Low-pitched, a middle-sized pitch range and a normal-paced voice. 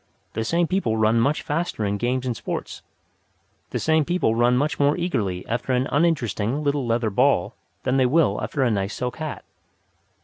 Yes: low, 125 Hz; average, 4.9 semitones; average, 180 wpm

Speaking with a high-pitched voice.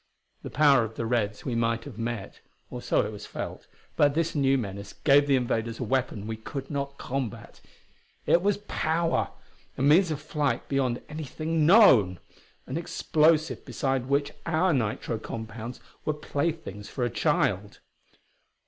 No: low, 135 Hz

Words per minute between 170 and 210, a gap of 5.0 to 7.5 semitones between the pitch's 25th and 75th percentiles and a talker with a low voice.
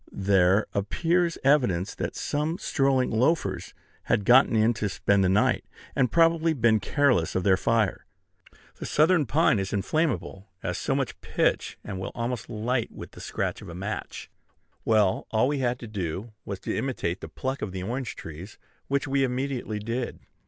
Yes: average, 175 wpm; wide, 5.6 semitones; low, 115 Hz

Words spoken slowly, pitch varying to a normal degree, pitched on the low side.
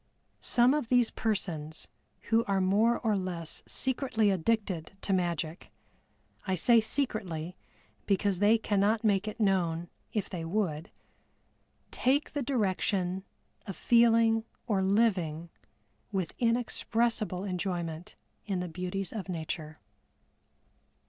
No: slow, 115 wpm; average, 4.2 semitones; high, 195 Hz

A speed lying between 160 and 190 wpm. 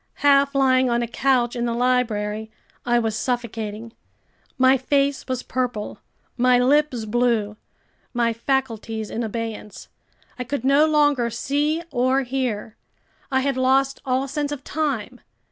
No: average, 140 wpm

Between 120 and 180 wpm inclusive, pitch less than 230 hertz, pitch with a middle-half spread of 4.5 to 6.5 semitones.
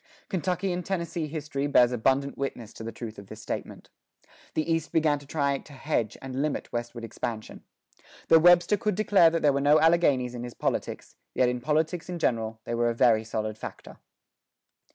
No: average, 190 wpm; medium, 140 Hz; wide, 5.5 semitones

